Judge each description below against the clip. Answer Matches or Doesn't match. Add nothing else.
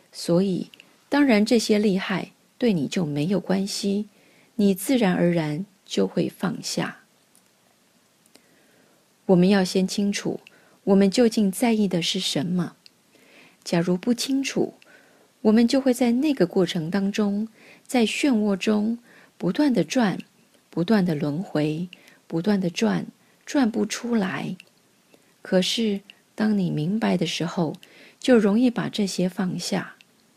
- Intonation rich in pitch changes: Doesn't match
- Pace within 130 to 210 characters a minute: Matches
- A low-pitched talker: Doesn't match